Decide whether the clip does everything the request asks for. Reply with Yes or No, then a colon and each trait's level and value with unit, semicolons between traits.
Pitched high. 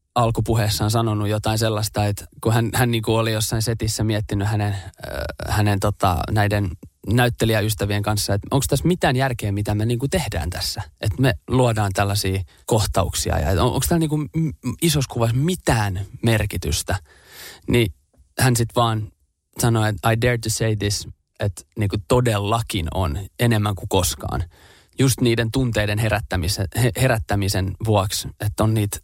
No: low, 110 Hz